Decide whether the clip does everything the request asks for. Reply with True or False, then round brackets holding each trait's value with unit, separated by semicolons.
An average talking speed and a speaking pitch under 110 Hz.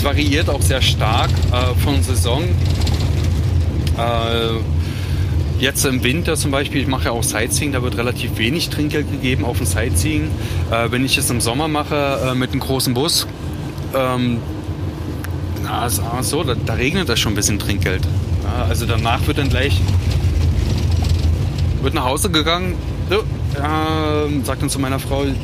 True (160 wpm; 100 Hz)